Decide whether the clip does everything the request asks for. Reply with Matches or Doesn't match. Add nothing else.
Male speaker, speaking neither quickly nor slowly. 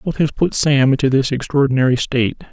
Matches